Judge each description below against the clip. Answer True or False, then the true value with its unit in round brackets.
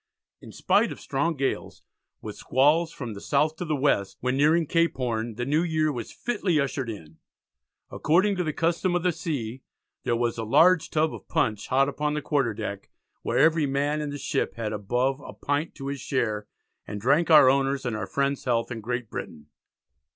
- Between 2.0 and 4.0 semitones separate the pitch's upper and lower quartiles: False (4.7 semitones)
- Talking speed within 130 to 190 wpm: False (200 wpm)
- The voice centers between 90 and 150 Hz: True (140 Hz)